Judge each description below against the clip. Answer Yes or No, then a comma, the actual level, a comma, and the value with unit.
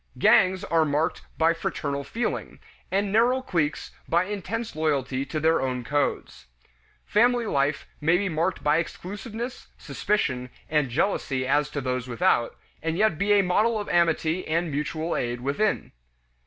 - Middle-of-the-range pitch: Yes, medium, 165 Hz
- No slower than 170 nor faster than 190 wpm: No, average, 150 wpm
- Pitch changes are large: Yes, wide, 6.0 semitones